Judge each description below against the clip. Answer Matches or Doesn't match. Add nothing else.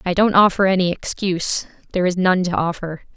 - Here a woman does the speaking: Matches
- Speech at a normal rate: Matches